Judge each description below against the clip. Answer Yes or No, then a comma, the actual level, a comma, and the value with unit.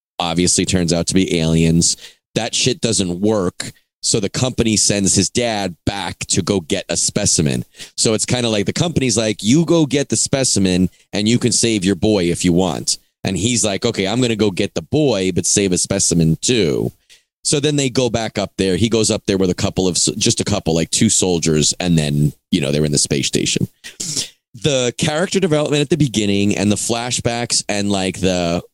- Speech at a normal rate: No, fast, 215 wpm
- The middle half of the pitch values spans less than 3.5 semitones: No, average, 4.9 semitones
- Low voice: Yes, low, 100 Hz